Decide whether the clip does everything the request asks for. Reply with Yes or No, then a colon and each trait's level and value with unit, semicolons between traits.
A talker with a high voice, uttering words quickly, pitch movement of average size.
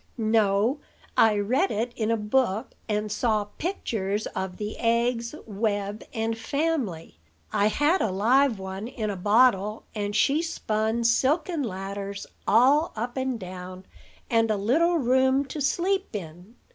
No: high, 225 Hz; average, 145 wpm; average, 4.4 semitones